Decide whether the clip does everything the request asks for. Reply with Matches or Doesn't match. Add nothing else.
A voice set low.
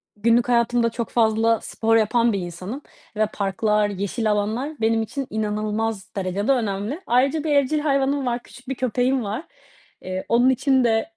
Doesn't match